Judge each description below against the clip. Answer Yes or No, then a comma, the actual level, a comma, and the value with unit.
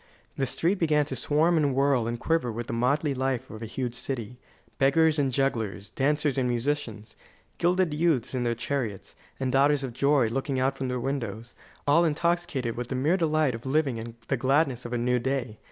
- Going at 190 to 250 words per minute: Yes, average, 200 wpm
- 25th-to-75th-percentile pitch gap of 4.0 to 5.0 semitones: No, average, 3.6 semitones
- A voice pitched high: No, low, 135 Hz